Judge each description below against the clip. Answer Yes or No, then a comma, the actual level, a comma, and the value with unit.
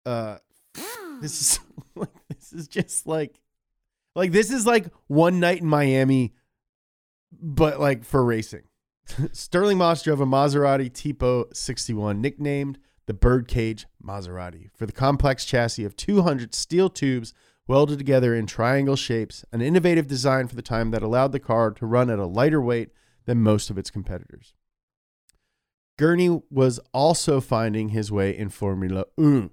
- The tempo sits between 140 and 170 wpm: Yes, average, 150 wpm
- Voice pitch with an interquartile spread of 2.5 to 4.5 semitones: No, average, 4.9 semitones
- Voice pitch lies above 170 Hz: No, low, 130 Hz